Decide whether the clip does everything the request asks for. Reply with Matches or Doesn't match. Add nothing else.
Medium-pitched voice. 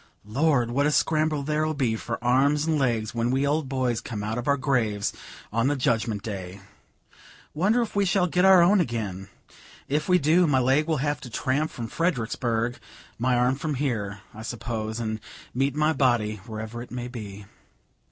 Doesn't match